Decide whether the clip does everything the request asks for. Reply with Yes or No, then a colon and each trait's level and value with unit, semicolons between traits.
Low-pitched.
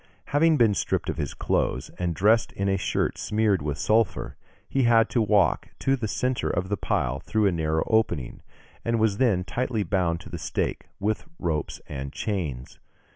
Yes: low, 100 Hz